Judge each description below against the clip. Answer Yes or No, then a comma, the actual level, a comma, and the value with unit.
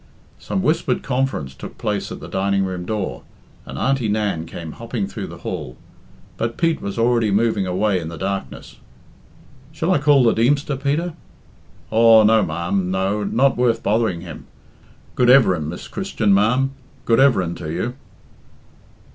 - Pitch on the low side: Yes, low, 110 Hz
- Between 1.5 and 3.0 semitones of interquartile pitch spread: No, average, 5.1 semitones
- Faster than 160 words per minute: No, average, 155 wpm